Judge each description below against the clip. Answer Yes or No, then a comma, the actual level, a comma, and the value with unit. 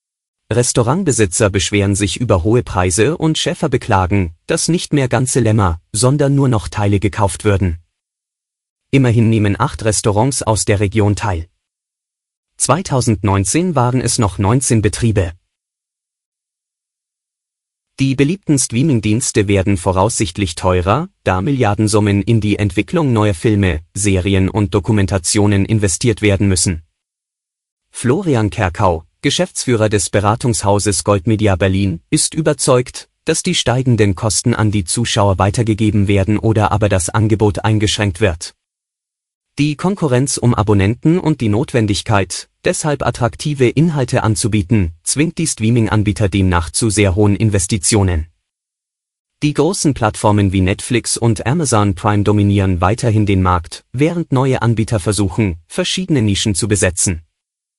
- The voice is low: Yes, low, 105 Hz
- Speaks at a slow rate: Yes, slow, 120 wpm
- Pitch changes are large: No, average, 3.7 semitones